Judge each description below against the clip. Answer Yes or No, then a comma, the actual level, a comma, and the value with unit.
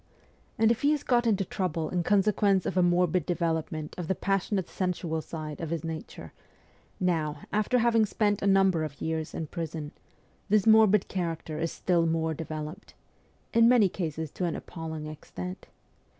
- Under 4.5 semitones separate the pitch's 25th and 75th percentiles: Yes, average, 3.8 semitones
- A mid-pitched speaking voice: Yes, medium, 175 Hz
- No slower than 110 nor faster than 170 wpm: Yes, average, 165 wpm